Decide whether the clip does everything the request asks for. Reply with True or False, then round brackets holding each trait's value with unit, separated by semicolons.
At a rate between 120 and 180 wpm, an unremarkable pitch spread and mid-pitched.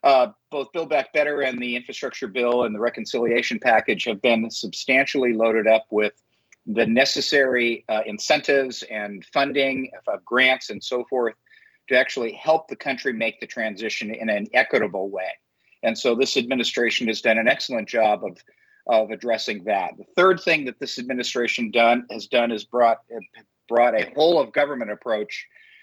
False (170 wpm; 3.8 semitones; 125 Hz)